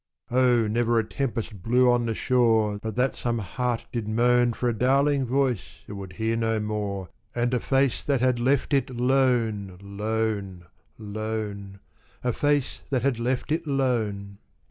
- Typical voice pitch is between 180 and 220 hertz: No, low, 115 Hz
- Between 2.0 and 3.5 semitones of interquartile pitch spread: Yes, average, 3.1 semitones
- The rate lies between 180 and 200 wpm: No, average, 165 wpm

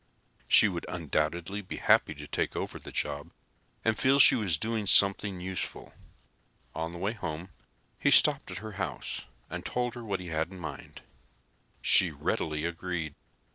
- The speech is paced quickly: No, average, 165 wpm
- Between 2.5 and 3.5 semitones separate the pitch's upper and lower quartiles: No, average, 4.2 semitones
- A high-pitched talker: No, very low, 90 Hz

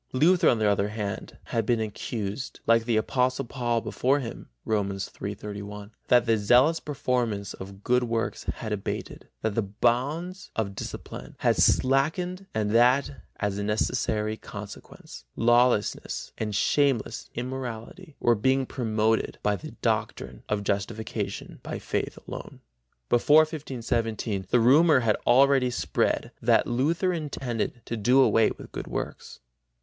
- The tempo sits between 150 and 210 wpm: No, average, 140 wpm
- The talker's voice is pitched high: No, low, 115 Hz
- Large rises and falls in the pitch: No, average, 3.7 semitones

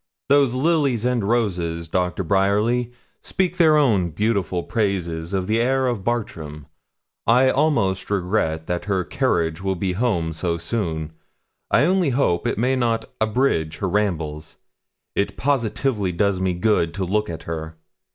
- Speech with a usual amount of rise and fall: No, wide, 5.8 semitones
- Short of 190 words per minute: Yes, average, 150 wpm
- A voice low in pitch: Yes, low, 100 Hz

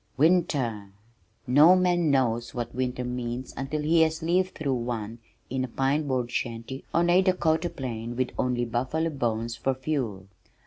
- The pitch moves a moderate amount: Yes, average, 4.9 semitones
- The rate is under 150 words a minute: No, average, 160 wpm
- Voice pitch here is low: Yes, low, 130 Hz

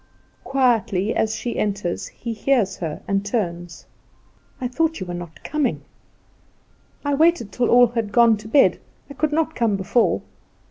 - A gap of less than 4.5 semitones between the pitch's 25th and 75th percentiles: No, average, 5.1 semitones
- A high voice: Yes, high, 230 Hz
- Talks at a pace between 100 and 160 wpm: Yes, average, 155 wpm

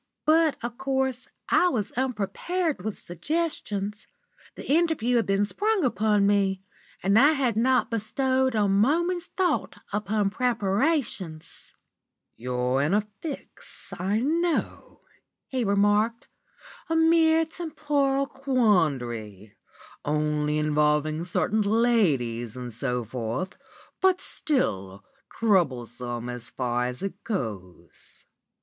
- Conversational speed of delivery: No, slow, 110 wpm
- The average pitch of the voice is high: Yes, high, 210 Hz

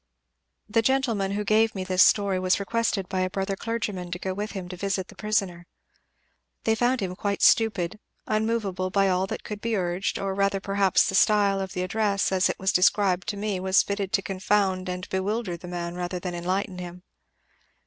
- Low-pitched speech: No, high, 195 Hz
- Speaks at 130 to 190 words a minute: No, average, 200 wpm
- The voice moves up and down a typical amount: No, narrow, 2.2 semitones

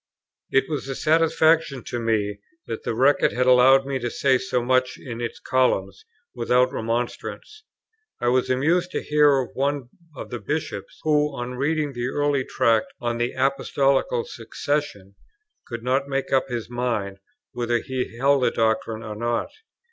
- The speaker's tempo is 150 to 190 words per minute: Yes, average, 165 wpm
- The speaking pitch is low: Yes, low, 130 Hz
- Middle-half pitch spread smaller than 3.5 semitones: Yes, average, 2.9 semitones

